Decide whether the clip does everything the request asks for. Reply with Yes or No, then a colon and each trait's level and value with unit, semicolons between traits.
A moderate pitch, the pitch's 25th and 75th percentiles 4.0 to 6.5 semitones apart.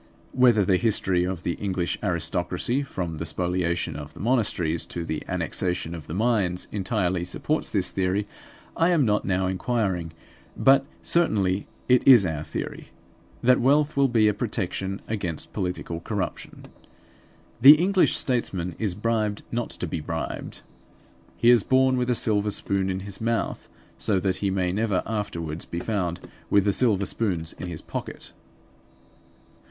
No: low, 100 Hz; average, 4.6 semitones